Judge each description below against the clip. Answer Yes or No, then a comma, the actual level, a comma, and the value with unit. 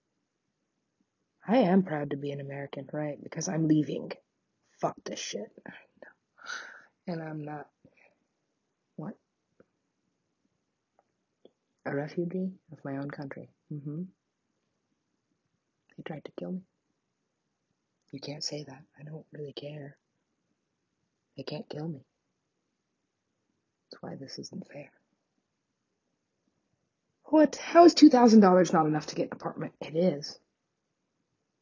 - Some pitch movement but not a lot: Yes, average, 4.1 semitones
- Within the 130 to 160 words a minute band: No, slow, 115 wpm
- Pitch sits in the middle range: Yes, medium, 155 Hz